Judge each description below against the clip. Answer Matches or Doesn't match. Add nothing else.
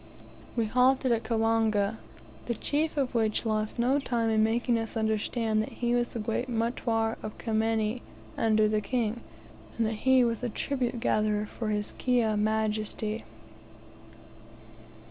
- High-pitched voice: Matches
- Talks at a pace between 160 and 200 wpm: Doesn't match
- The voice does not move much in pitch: Matches